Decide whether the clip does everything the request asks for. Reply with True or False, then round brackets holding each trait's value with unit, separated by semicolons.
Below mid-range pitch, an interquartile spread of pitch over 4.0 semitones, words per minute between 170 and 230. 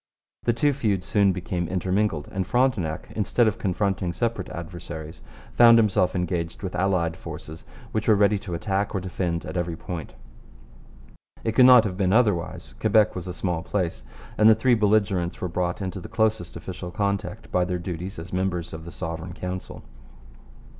False (95 Hz; 3.3 semitones; 175 wpm)